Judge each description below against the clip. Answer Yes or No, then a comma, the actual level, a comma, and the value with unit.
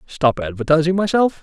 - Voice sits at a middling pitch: Yes, medium, 160 Hz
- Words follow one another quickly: No, slow, 125 wpm